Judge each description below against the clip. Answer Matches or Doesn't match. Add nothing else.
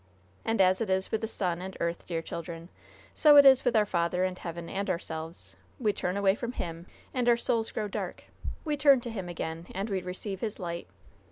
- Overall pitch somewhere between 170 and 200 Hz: Matches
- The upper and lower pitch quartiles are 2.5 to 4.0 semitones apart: Doesn't match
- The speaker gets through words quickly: Matches